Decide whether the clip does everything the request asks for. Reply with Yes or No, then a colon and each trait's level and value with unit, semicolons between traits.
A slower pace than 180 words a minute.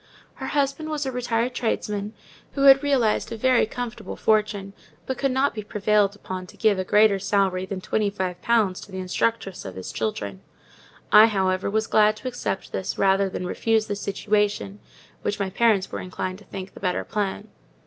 No: average, 185 wpm